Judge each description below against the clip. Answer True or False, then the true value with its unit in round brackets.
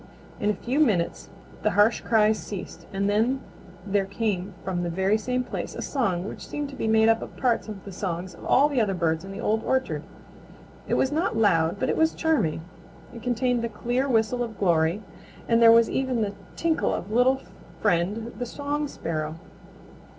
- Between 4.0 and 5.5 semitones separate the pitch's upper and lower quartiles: True (4.5 semitones)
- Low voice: False (220 Hz)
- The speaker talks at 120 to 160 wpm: False (195 wpm)